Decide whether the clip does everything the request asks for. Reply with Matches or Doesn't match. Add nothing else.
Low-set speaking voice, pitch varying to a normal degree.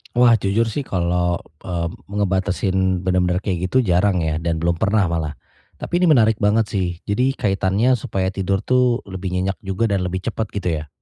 Matches